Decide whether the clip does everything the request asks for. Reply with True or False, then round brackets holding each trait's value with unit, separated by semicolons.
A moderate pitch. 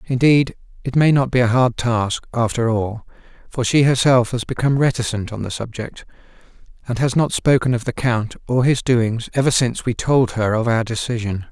False (120 Hz)